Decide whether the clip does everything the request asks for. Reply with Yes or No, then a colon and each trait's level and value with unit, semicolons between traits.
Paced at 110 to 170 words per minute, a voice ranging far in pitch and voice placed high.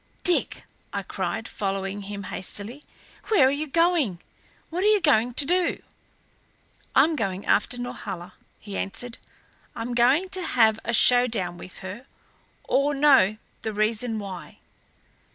Yes: slow, 135 wpm; wide, 6.2 semitones; high, 235 Hz